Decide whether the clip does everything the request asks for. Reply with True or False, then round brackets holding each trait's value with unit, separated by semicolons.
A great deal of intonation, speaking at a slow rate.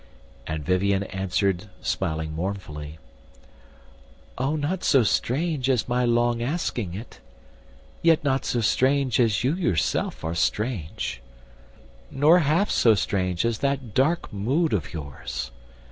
True (6.9 semitones; 125 wpm)